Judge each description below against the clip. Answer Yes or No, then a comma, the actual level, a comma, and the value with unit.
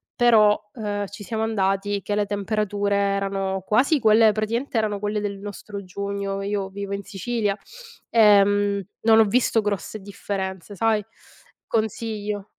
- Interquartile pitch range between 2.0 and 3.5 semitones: No, narrow, 1.5 semitones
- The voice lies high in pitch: Yes, high, 205 Hz